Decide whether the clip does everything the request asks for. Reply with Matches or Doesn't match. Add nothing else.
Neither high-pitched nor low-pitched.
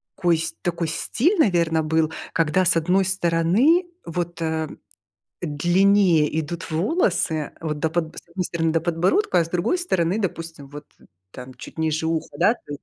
Matches